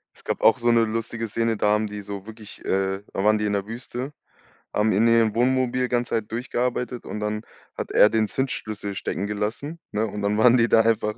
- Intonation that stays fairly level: Yes, narrow, 2.3 semitones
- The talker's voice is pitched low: Yes, low, 110 Hz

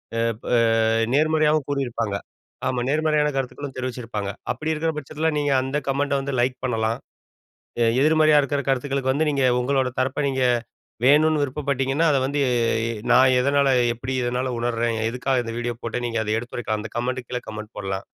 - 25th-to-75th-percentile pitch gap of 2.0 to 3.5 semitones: Yes, average, 3.0 semitones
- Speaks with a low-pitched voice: Yes, low, 130 Hz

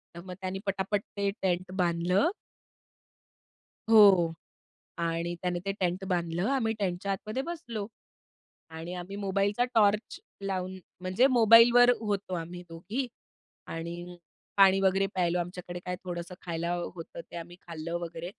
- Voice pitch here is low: No, medium, 185 Hz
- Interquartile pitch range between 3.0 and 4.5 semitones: No, narrow, 2.6 semitones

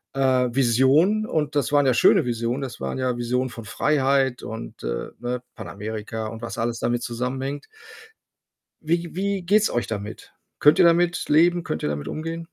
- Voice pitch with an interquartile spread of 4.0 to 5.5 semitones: Yes, average, 5.1 semitones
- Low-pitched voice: Yes, low, 130 Hz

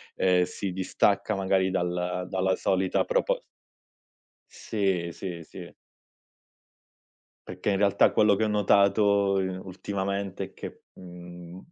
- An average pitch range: No, narrow, 1.8 semitones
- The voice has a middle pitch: No, very low, 95 Hz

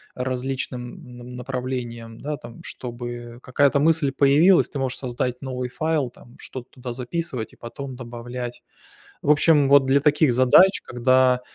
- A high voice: No, low, 130 Hz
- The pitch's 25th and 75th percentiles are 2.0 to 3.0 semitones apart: Yes, narrow, 2.4 semitones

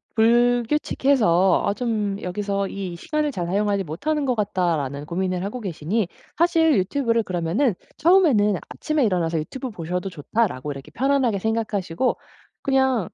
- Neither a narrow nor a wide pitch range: No, wide, 6.0 semitones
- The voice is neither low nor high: No, high, 205 Hz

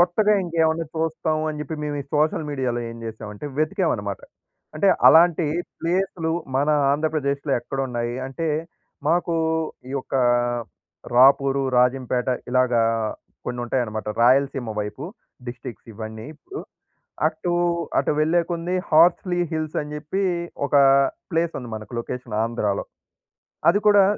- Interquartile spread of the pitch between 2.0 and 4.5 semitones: No, average, 4.9 semitones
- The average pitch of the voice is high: No, medium, 145 Hz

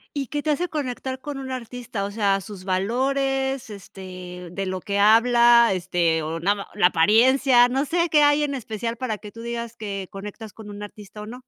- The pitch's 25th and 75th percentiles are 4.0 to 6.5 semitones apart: Yes, average, 4.8 semitones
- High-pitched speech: Yes, high, 225 Hz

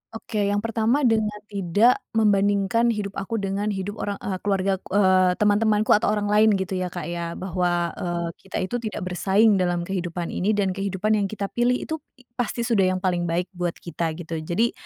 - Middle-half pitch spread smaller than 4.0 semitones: Yes, average, 2.8 semitones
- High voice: Yes, high, 195 Hz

